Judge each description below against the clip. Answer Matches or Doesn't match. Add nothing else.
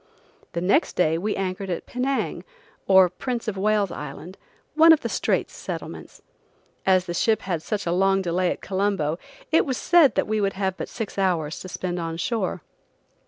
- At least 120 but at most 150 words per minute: Doesn't match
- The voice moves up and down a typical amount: Matches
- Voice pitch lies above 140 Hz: Matches